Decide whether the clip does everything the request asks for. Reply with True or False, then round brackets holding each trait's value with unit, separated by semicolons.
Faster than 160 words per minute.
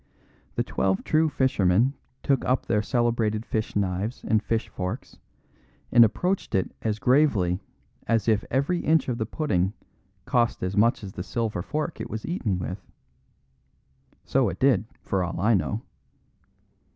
False (150 wpm)